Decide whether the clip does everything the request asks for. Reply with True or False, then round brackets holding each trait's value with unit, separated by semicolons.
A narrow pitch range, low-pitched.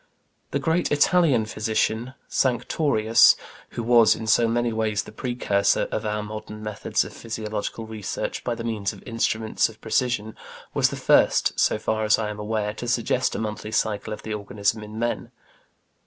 True (1.8 semitones; 110 Hz)